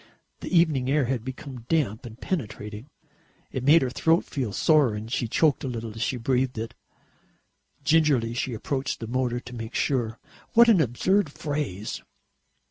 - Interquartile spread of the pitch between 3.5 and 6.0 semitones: Yes, average, 4.5 semitones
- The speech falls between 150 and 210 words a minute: Yes, average, 165 wpm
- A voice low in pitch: Yes, low, 130 Hz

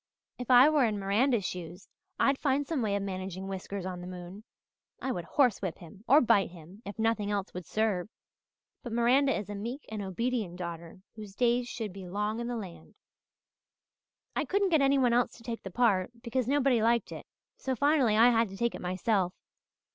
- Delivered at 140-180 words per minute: No, average, 200 wpm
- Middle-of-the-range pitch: No, high, 220 Hz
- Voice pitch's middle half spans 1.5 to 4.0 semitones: No, average, 4.6 semitones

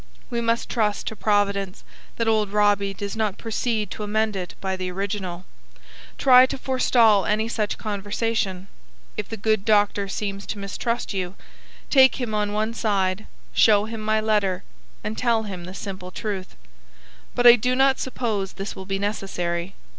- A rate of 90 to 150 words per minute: No, average, 165 wpm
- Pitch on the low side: No, high, 210 Hz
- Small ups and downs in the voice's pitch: Yes, narrow, 2.3 semitones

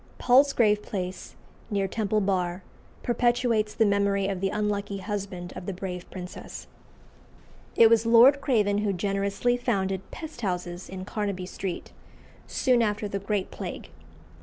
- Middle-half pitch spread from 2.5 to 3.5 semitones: Yes, average, 2.9 semitones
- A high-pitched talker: Yes, high, 200 Hz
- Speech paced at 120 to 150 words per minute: Yes, slow, 135 wpm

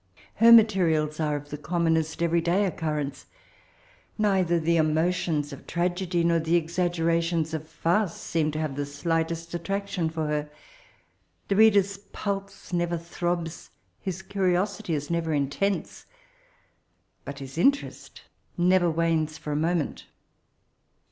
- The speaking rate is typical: No, slow, 130 wpm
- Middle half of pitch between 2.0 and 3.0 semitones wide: Yes, narrow, 2.5 semitones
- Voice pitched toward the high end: No, medium, 170 Hz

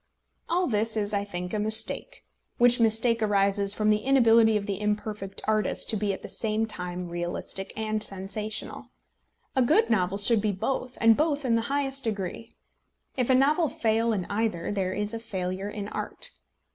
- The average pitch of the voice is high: Yes, high, 215 Hz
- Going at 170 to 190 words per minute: Yes, average, 180 wpm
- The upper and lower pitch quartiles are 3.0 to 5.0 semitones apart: No, narrow, 2.6 semitones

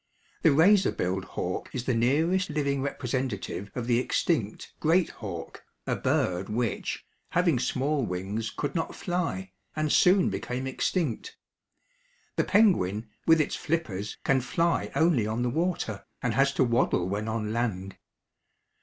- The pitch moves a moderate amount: No, wide, 7.1 semitones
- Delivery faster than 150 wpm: No, average, 145 wpm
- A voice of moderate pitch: No, low, 125 Hz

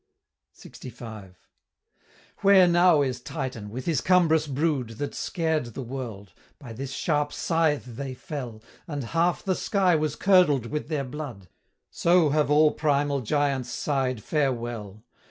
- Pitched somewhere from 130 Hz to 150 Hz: Yes, medium, 140 Hz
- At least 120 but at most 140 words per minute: Yes, slow, 135 wpm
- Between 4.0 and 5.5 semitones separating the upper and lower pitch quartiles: Yes, average, 4.4 semitones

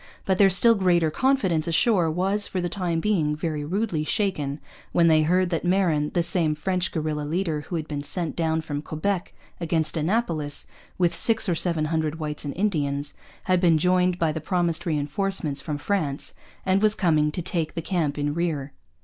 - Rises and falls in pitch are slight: No, average, 3.3 semitones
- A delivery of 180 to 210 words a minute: Yes, average, 185 wpm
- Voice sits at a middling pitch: Yes, medium, 165 Hz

